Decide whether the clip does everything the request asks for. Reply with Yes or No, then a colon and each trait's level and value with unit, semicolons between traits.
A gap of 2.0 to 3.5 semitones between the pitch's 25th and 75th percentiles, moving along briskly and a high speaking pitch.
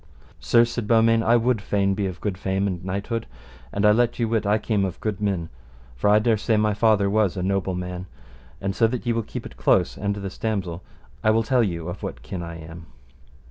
No: average, 3.1 semitones; fast, 240 wpm; low, 100 Hz